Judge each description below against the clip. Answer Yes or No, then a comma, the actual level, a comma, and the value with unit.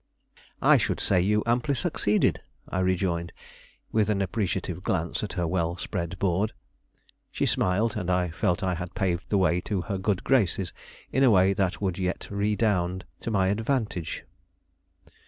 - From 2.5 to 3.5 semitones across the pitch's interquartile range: Yes, average, 2.8 semitones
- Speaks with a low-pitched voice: Yes, very low, 95 Hz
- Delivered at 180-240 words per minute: No, average, 160 wpm